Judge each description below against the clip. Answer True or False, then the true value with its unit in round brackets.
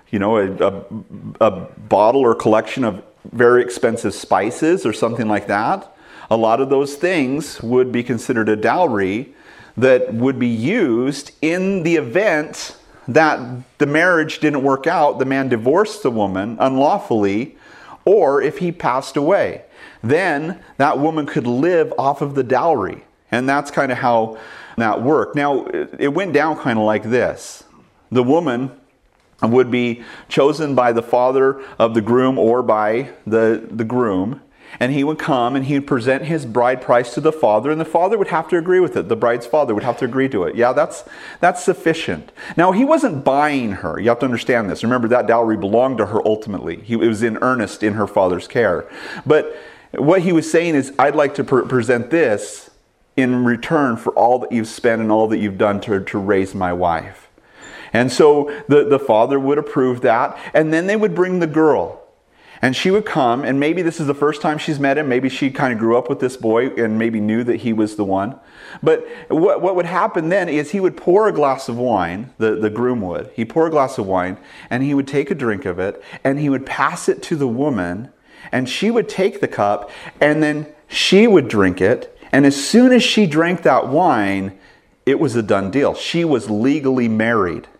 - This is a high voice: False (135 Hz)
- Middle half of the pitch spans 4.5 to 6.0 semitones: True (5.1 semitones)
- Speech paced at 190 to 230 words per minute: True (205 wpm)